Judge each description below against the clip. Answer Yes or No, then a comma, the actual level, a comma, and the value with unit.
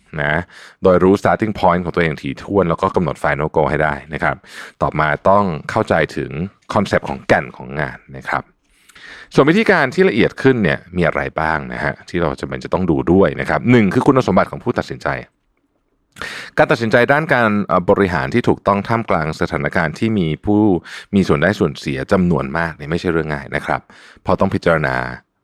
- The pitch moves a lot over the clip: Yes, wide, 6.2 semitones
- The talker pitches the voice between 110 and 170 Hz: No, very low, 85 Hz